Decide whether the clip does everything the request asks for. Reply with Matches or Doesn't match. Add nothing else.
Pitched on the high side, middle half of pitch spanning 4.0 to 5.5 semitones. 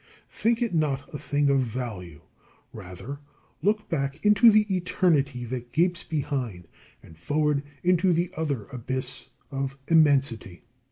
Doesn't match